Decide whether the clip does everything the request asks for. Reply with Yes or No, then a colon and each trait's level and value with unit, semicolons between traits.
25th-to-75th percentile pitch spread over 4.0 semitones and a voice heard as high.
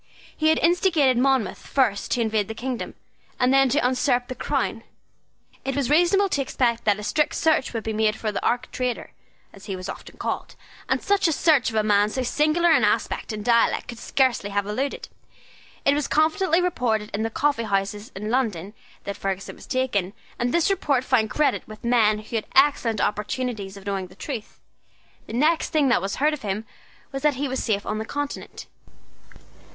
Yes: average, 5.1 semitones; high, 245 Hz